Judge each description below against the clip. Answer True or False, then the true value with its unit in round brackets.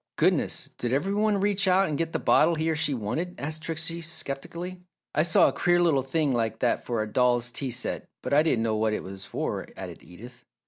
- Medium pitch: True (150 Hz)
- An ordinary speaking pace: False (225 wpm)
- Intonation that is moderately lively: False (5.9 semitones)